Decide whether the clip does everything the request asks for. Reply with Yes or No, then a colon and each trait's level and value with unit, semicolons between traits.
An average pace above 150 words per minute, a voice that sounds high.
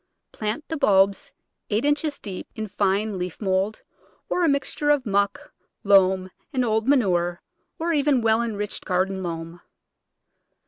No: average, 140 wpm; high, 210 Hz